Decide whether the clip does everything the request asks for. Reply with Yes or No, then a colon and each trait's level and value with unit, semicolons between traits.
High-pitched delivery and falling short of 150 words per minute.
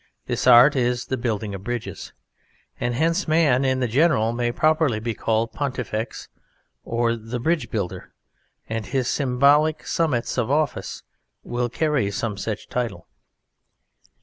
No: low, 120 Hz; average, 140 wpm